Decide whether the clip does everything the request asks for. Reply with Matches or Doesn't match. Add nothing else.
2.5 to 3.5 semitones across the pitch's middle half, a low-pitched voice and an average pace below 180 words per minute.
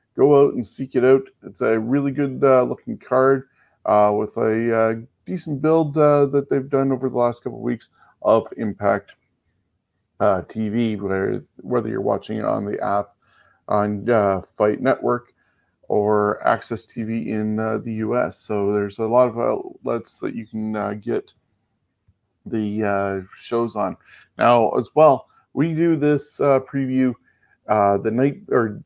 Doesn't match